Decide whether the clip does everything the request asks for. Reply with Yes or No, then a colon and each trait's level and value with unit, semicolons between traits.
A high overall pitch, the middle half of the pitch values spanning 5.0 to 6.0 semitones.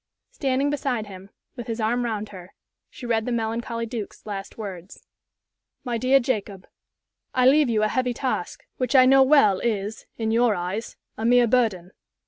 No: high, 230 Hz; average, 3.3 semitones